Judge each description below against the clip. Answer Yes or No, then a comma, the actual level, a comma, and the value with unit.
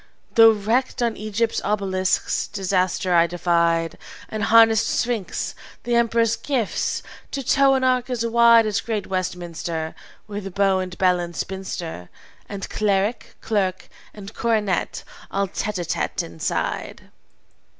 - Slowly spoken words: Yes, slow, 130 wpm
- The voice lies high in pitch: Yes, high, 200 Hz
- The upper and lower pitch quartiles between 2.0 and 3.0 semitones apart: No, average, 3.9 semitones